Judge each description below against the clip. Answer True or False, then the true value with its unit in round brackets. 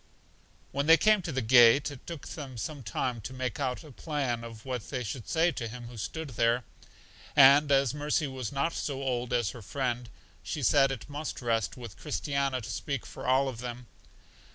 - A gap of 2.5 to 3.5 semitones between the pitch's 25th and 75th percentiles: True (3.1 semitones)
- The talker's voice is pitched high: False (130 Hz)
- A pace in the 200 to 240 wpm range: True (205 wpm)